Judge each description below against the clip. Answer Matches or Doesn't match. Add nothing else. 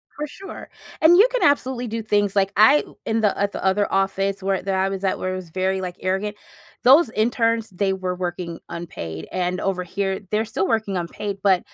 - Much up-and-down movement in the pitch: Doesn't match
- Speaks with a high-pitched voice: Matches